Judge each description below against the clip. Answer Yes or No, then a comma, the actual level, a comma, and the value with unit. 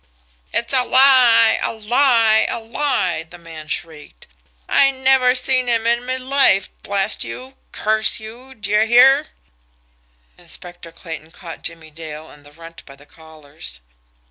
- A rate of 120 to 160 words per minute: Yes, average, 145 wpm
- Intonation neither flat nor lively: No, wide, 7.5 semitones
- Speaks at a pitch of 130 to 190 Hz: No, high, 220 Hz